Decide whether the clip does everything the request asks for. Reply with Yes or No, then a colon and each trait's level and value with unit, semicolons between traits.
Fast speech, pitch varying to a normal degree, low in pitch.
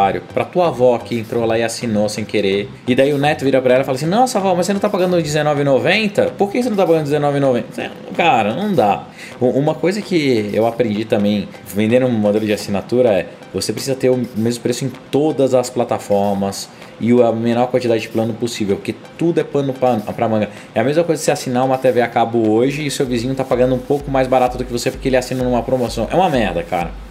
Yes: fast, 235 wpm; average, 3.9 semitones; low, 125 Hz